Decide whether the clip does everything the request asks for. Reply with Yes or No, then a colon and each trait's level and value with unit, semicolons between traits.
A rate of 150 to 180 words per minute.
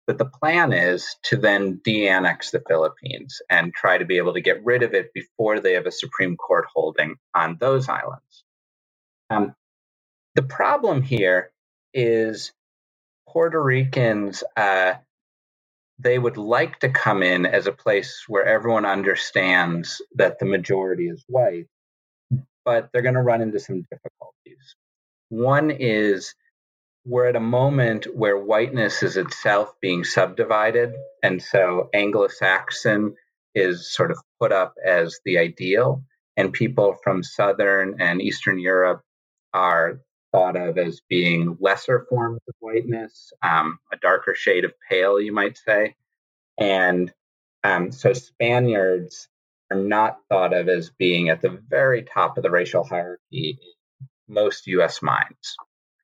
No: average, 140 wpm